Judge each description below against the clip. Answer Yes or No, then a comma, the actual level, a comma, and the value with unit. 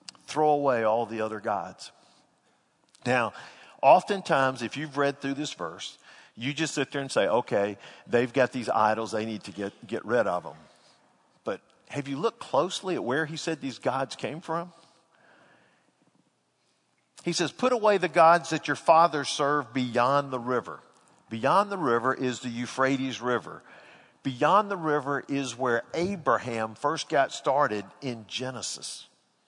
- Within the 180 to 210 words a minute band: No, average, 155 wpm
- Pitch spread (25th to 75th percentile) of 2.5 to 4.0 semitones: No, average, 4.9 semitones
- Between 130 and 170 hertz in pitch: Yes, low, 135 Hz